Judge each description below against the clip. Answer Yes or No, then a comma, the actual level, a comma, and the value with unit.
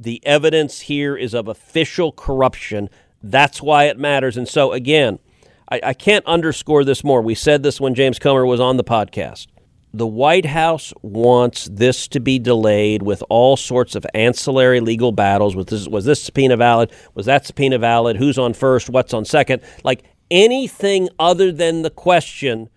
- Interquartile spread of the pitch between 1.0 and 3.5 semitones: No, average, 4.1 semitones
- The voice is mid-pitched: No, low, 130 Hz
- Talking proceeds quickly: No, average, 175 wpm